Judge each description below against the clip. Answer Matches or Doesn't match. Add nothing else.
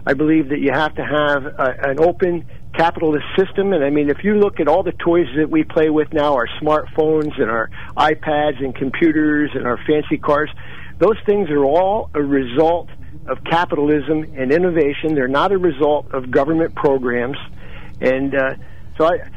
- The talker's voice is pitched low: Doesn't match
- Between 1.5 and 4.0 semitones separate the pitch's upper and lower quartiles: Matches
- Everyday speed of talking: Matches